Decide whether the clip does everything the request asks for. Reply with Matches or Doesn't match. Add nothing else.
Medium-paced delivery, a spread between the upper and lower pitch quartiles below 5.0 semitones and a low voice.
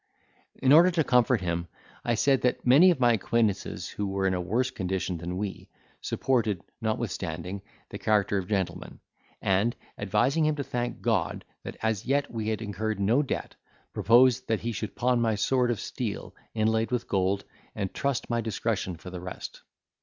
Matches